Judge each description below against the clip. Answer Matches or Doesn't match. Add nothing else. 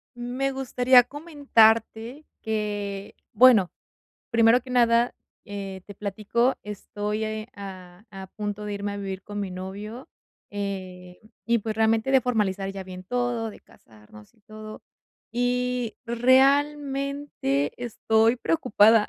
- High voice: Matches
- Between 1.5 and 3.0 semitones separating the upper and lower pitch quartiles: Doesn't match